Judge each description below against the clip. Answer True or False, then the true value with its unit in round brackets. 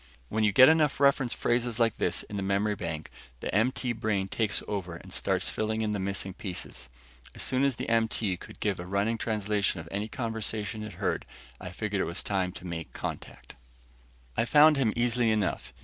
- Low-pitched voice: True (105 Hz)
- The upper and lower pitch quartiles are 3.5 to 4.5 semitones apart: False (3.1 semitones)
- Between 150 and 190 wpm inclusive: False (200 wpm)